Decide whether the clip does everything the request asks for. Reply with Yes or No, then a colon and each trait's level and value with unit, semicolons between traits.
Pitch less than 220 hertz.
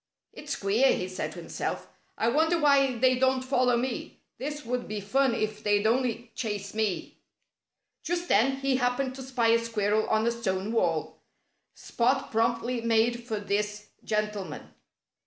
No: high, 235 Hz